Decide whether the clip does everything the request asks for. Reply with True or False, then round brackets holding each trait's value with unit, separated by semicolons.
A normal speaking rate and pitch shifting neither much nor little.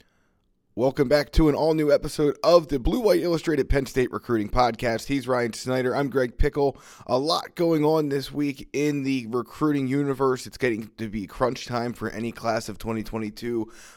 True (185 wpm; 4.0 semitones)